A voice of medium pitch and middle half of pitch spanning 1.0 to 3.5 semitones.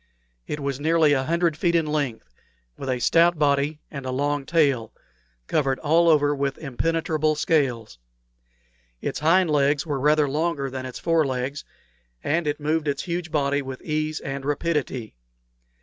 Yes: medium, 145 Hz; narrow, 2.6 semitones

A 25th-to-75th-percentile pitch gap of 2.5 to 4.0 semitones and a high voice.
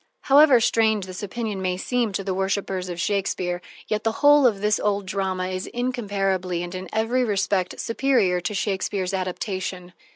Yes: average, 3.1 semitones; high, 195 Hz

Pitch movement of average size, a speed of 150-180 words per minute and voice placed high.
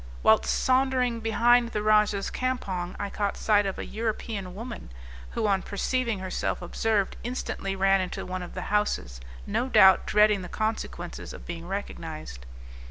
Yes: average, 3.5 semitones; average, 155 wpm; high, 205 Hz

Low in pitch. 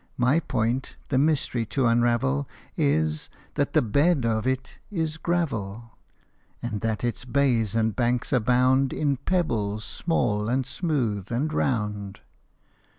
Yes: low, 120 Hz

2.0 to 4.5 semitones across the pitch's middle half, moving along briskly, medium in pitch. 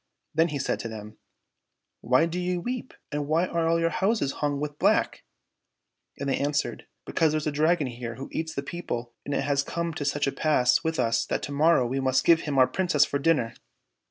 Yes: average, 3.7 semitones; fast, 235 wpm; medium, 145 Hz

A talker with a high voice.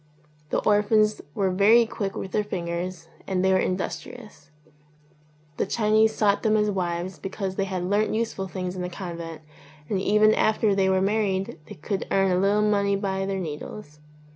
Yes: high, 195 Hz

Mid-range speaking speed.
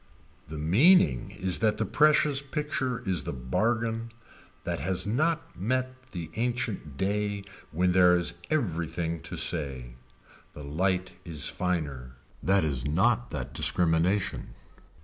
No: slow, 130 wpm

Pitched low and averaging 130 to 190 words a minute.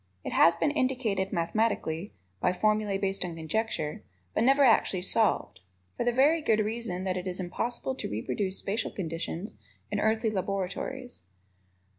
No: high, 205 Hz; average, 150 wpm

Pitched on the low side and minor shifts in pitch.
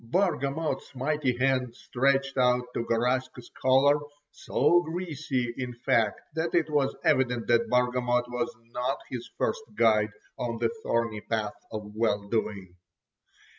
No: low, 125 Hz; average, 3.0 semitones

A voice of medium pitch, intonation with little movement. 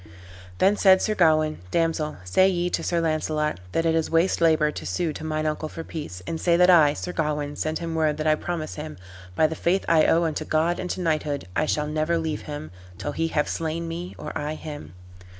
Yes: medium, 160 Hz; narrow, 1.7 semitones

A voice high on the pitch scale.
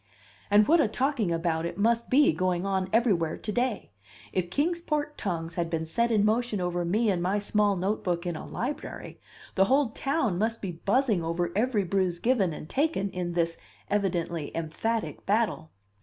Yes: high, 195 Hz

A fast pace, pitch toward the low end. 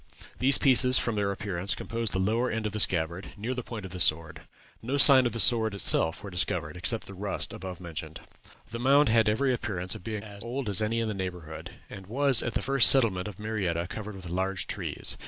Yes: fast, 225 wpm; low, 105 Hz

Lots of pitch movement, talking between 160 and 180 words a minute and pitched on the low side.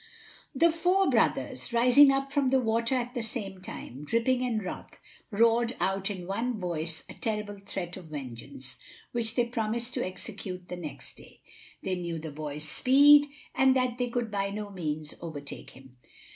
No: wide, 6.2 semitones; average, 170 wpm; high, 210 Hz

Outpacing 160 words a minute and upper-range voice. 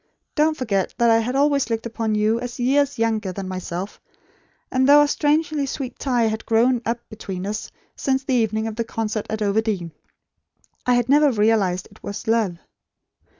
Yes: average, 180 wpm; high, 225 Hz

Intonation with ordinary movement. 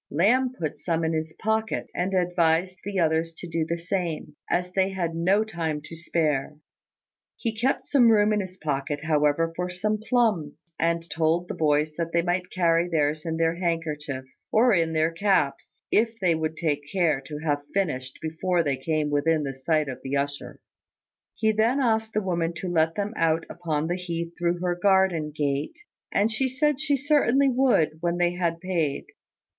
Yes: average, 3.6 semitones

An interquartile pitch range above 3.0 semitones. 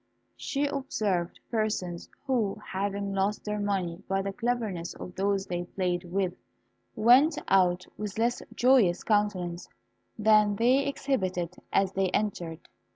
Yes: average, 3.4 semitones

